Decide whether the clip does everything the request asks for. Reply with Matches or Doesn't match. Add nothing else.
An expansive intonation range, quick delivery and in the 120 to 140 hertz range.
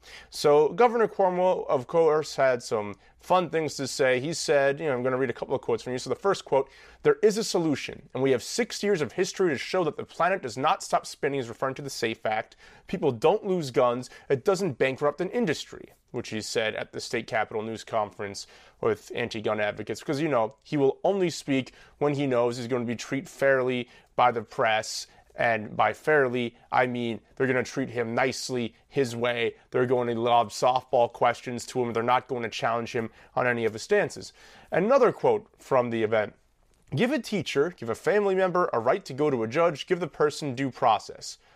Matches